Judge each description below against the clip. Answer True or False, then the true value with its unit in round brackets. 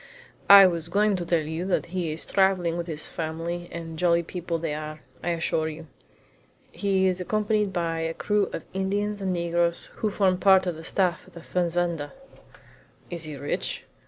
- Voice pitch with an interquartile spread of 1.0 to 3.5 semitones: True (2.6 semitones)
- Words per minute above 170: True (190 wpm)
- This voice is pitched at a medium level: True (175 Hz)